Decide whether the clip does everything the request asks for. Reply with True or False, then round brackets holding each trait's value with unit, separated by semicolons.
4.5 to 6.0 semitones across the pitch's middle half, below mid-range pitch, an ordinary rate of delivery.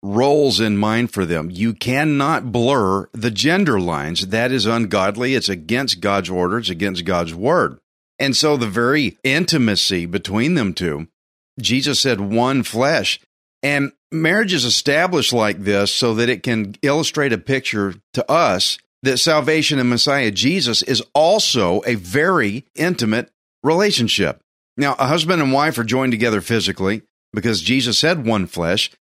True (5.1 semitones; 120 Hz; 155 wpm)